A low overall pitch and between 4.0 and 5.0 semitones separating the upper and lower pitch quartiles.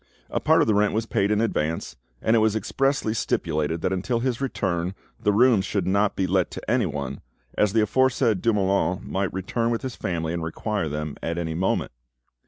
Yes: low, 100 Hz; average, 4.6 semitones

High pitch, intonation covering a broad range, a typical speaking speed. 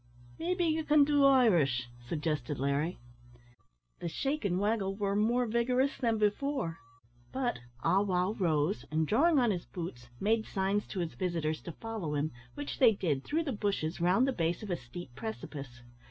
Yes: high, 195 Hz; wide, 7.1 semitones; average, 170 wpm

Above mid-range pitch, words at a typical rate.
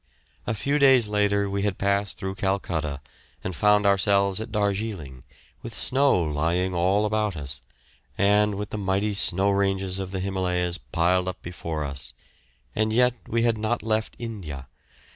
No: low, 100 Hz; average, 160 wpm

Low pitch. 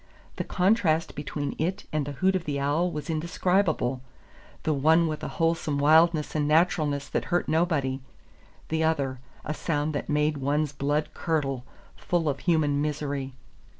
No: medium, 155 Hz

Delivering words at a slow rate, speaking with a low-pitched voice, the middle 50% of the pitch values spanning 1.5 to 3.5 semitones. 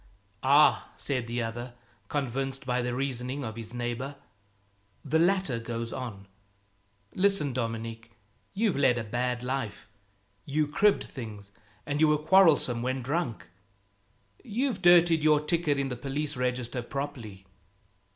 No: slow, 130 wpm; low, 130 Hz; average, 4.0 semitones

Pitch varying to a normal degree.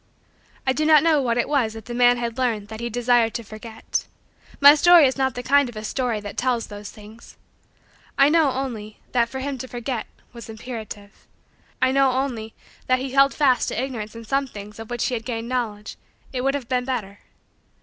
Yes: average, 3.0 semitones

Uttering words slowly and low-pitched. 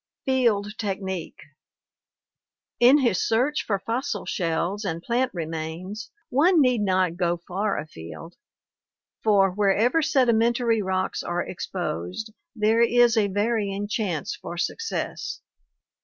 No: slow, 110 wpm; high, 205 Hz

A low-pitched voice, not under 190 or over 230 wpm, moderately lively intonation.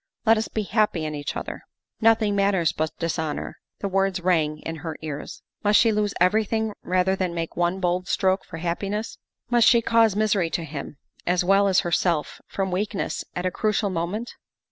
No: high, 190 Hz; average, 195 wpm; average, 3.6 semitones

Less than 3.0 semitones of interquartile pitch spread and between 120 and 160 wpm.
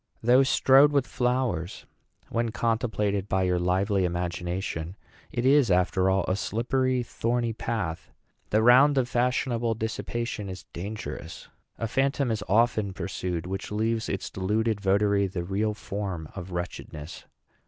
No: average, 4.2 semitones; slow, 135 wpm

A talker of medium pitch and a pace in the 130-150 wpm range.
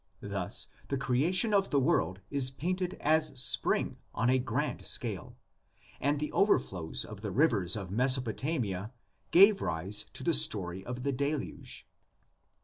No: low, 130 Hz; average, 140 wpm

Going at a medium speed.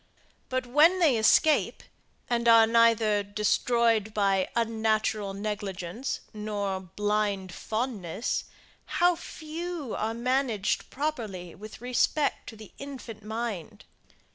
No: slow, 105 wpm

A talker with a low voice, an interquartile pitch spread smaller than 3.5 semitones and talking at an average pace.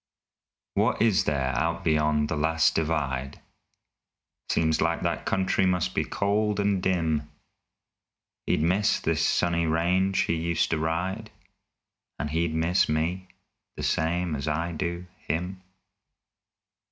No: very low, 85 Hz; average, 2.8 semitones; slow, 130 wpm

